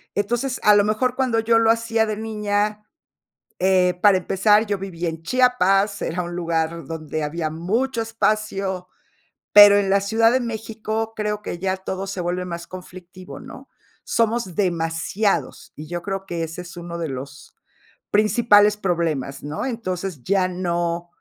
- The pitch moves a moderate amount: Yes, average, 3.9 semitones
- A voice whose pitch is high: Yes, high, 195 Hz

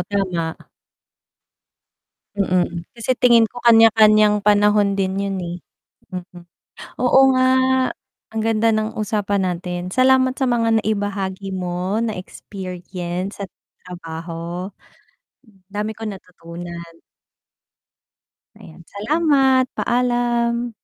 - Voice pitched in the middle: No, high, 205 Hz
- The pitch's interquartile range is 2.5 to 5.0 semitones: Yes, average, 4.1 semitones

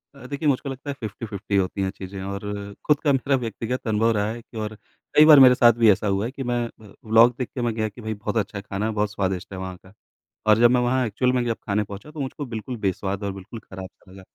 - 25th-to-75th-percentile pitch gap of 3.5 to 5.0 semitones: Yes, average, 3.9 semitones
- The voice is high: No, low, 110 Hz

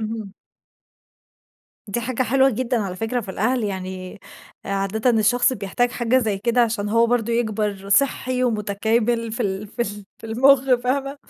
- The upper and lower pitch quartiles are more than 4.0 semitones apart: No, average, 3.2 semitones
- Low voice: No, high, 225 Hz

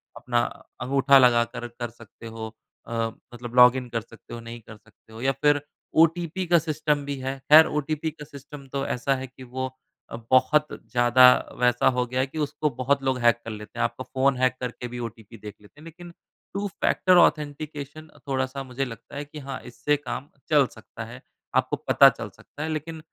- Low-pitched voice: Yes, low, 130 Hz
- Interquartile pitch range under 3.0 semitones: No, average, 3.5 semitones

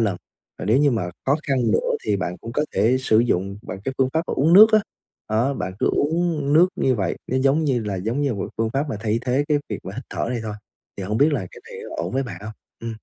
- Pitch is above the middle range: No, low, 120 Hz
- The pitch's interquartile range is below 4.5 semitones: No, average, 5.1 semitones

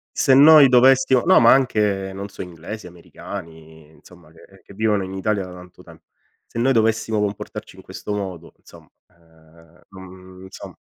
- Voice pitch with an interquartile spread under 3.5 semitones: No, average, 4.2 semitones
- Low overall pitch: Yes, very low, 95 Hz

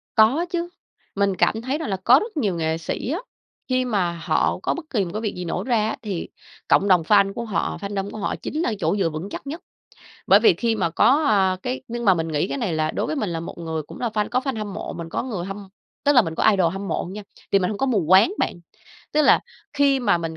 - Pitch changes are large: Yes, wide, 5.9 semitones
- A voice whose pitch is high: Yes, high, 205 Hz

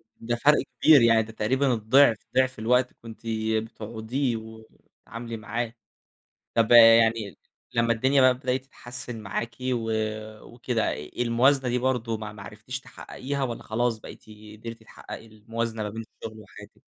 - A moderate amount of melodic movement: No, narrow, 2.2 semitones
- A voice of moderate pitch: No, low, 115 Hz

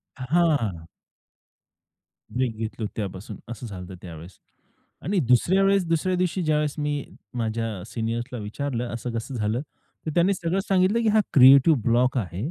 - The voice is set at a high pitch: No, low, 125 Hz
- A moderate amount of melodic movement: No, wide, 6.9 semitones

